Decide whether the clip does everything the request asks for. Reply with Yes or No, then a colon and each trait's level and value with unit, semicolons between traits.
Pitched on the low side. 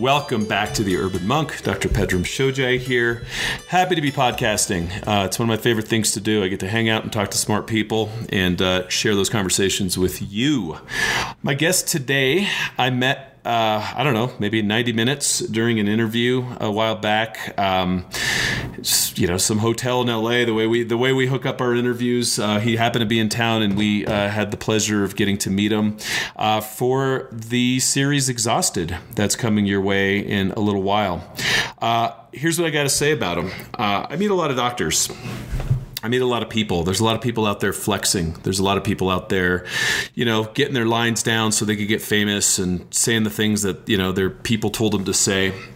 Yes: low, 110 Hz